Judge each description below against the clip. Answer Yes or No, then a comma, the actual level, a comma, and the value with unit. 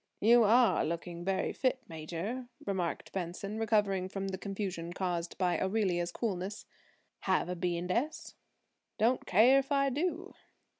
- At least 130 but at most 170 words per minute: Yes, average, 145 wpm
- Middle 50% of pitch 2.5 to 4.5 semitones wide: No, average, 5.0 semitones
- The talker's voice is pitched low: No, high, 195 Hz